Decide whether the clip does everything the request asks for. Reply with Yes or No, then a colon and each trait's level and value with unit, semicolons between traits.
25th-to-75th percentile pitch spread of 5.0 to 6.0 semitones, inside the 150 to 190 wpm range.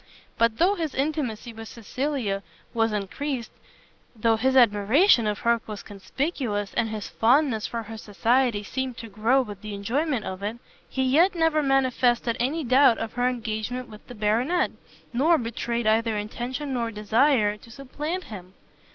No: average, 3.8 semitones; average, 160 wpm